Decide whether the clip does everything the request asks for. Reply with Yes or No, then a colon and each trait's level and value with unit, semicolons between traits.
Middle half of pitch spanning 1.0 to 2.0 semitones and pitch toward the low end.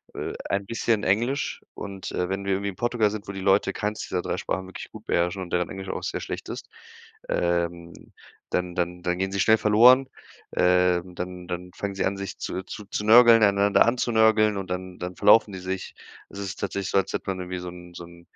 No: narrow, 2.6 semitones; very low, 95 Hz